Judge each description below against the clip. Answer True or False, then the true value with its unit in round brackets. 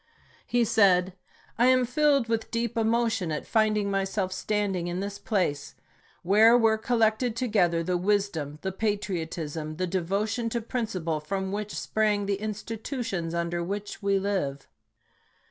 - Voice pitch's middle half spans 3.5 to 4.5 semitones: True (3.8 semitones)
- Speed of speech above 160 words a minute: False (145 wpm)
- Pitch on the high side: True (200 Hz)